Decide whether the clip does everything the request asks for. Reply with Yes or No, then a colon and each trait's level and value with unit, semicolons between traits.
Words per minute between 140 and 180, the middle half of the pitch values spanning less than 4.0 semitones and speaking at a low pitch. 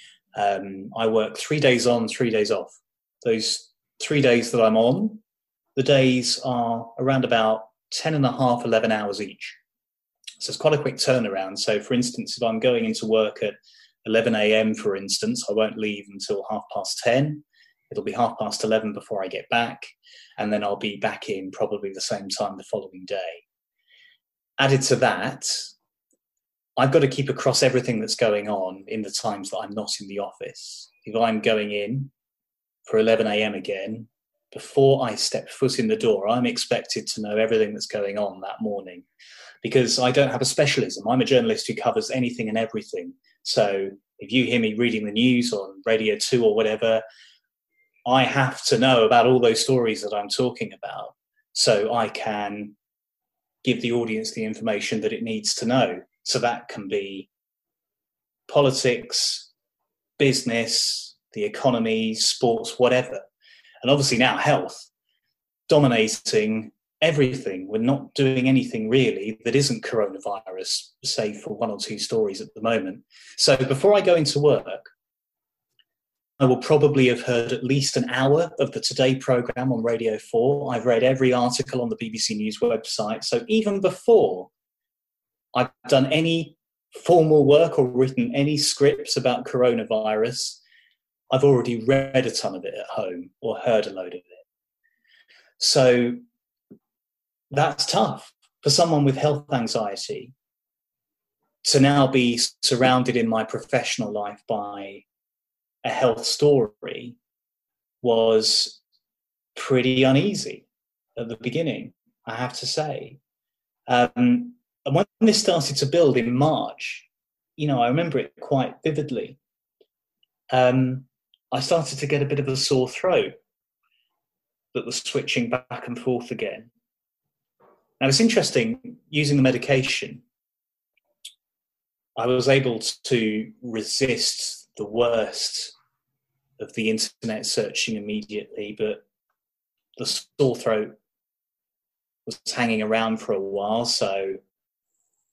No: average, 150 wpm; average, 5.0 semitones; low, 130 Hz